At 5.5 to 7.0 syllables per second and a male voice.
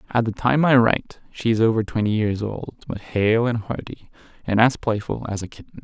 No: 5.2 syllables/s; male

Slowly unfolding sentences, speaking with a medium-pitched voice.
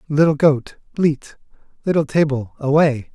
Yes: slow, 115 wpm; medium, 145 Hz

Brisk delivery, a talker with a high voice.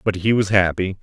No: fast, 235 wpm; very low, 95 Hz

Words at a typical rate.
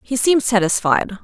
Yes: average, 145 wpm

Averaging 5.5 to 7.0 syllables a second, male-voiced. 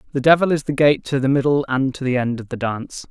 Yes: 6.4 syllables/s; male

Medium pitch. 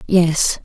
Yes: medium, 175 Hz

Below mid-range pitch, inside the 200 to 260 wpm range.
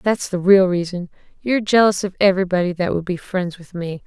No: medium, 185 Hz; fast, 205 wpm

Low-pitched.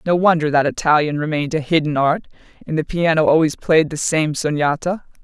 No: medium, 155 Hz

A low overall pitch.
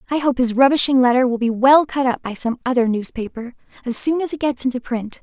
No: very high, 255 Hz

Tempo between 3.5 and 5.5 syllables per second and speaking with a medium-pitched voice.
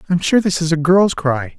Yes: 5.0 syllables/s; medium, 165 Hz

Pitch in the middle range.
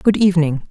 Yes: medium, 175 Hz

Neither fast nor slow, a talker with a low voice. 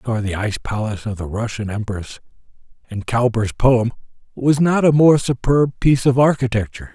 Yes: average, 180 wpm; low, 120 Hz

